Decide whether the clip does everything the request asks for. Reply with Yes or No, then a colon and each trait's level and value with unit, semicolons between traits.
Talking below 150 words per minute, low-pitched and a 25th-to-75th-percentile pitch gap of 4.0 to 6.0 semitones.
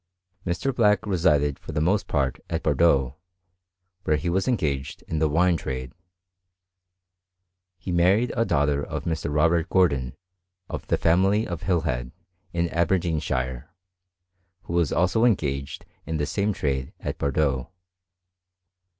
Yes: slow, 135 wpm; very low, 80 Hz; average, 4.4 semitones